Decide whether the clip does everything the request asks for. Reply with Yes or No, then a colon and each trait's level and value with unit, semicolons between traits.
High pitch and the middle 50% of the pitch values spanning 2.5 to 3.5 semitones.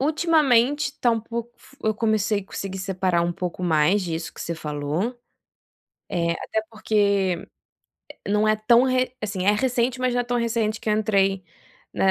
No: high, 215 Hz; average, 4.2 semitones